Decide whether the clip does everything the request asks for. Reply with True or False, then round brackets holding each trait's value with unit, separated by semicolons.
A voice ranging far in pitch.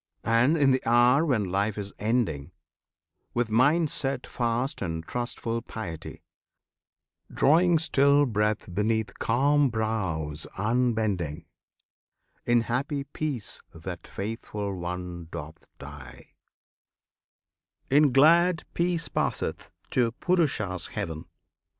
True (6.4 semitones)